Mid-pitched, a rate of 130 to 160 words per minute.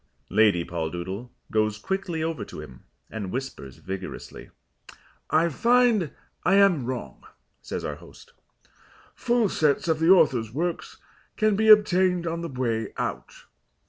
Yes: medium, 155 Hz; slow, 135 wpm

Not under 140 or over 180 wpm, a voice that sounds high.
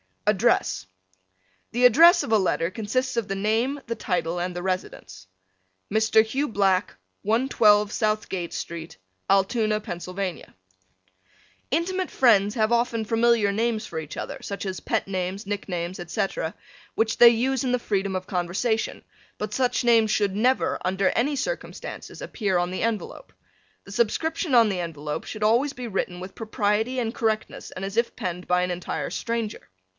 Yes: average, 160 wpm; high, 215 Hz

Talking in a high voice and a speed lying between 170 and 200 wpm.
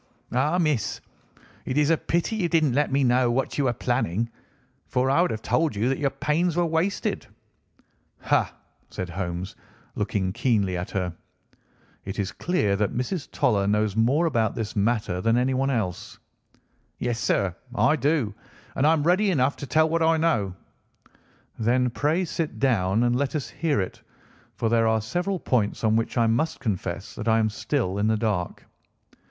No: low, 120 Hz; average, 180 wpm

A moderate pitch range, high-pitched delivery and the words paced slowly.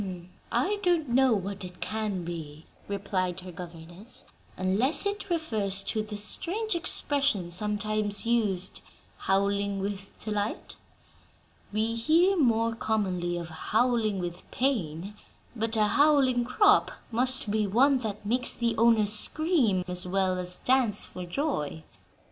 Yes: average, 5.0 semitones; high, 215 Hz; slow, 130 wpm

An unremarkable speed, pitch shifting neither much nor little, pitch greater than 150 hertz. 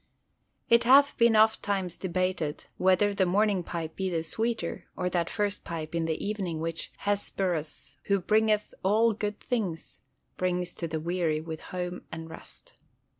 Yes: average, 155 wpm; average, 3.9 semitones; medium, 185 Hz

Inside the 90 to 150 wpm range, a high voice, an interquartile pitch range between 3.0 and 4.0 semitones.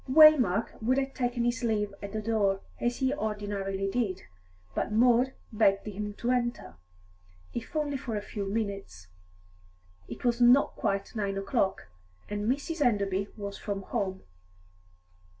Yes: average, 145 wpm; high, 215 Hz; average, 3.6 semitones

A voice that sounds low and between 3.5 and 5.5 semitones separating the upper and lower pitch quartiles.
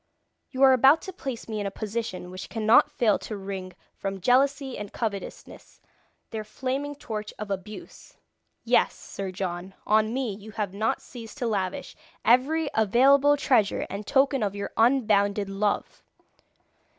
No: high, 220 Hz; average, 4.7 semitones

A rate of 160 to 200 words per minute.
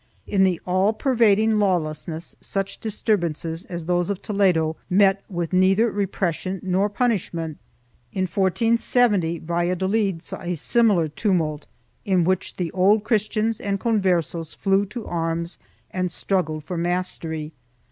No: slow, 135 wpm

